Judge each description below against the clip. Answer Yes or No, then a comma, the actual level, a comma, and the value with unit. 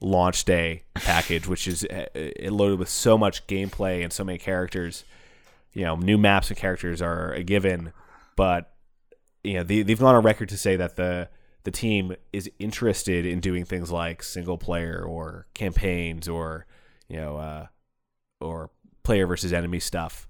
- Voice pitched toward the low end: Yes, very low, 90 Hz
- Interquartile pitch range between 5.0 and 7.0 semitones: No, narrow, 2.6 semitones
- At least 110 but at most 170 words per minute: Yes, average, 165 wpm